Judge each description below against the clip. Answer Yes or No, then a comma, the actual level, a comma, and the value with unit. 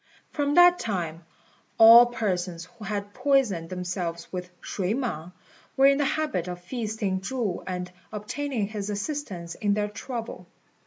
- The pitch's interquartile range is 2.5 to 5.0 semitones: No, wide, 5.4 semitones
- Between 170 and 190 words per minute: No, average, 145 wpm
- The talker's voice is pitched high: Yes, high, 205 Hz